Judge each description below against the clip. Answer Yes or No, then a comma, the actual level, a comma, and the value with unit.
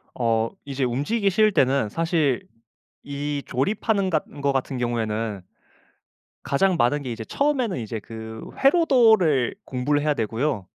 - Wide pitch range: Yes, wide, 7.6 semitones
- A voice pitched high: No, medium, 140 Hz